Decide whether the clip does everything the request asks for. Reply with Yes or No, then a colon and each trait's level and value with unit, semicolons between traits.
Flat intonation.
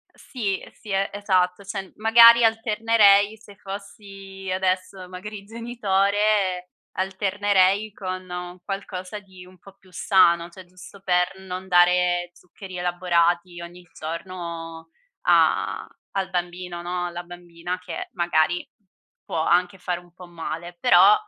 Yes: narrow, 2.0 semitones